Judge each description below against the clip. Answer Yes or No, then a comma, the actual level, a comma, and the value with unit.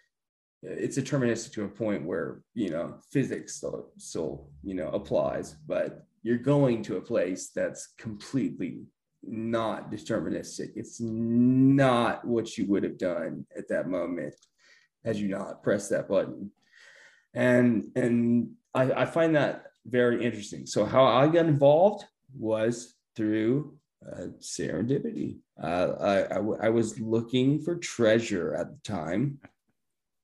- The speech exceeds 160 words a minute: No, slow, 135 wpm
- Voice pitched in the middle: No, low, 120 Hz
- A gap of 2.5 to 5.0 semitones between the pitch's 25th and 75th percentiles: Yes, average, 3.4 semitones